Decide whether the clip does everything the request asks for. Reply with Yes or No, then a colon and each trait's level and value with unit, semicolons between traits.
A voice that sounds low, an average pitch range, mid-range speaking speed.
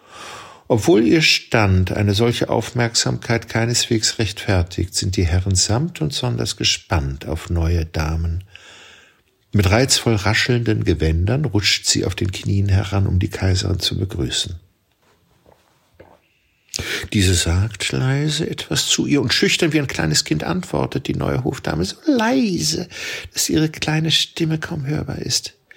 No: low, 110 Hz; wide, 6.5 semitones; average, 135 wpm